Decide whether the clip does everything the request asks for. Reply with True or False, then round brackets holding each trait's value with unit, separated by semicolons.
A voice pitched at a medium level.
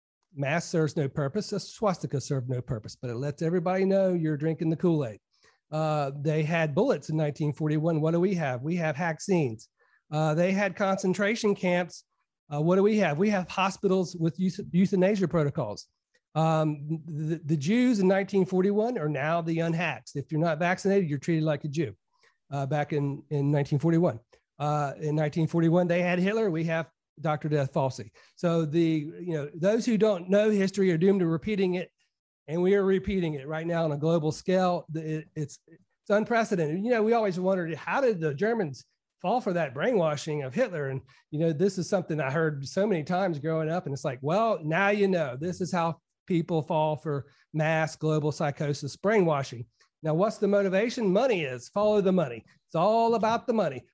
True (165 Hz)